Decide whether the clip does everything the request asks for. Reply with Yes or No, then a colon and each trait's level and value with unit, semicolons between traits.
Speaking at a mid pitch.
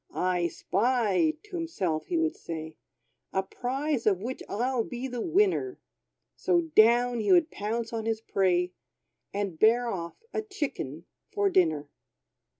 No: high, 225 Hz